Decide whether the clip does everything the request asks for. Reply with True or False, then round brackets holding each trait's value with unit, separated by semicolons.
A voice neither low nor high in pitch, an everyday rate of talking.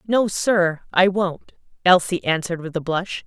True (180 Hz; 165 wpm)